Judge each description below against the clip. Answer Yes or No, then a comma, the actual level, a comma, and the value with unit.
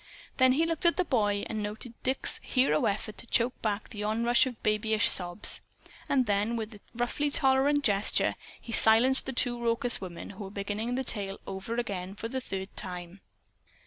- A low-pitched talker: No, high, 225 Hz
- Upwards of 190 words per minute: No, average, 185 wpm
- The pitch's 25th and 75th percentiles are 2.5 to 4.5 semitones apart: Yes, average, 3.9 semitones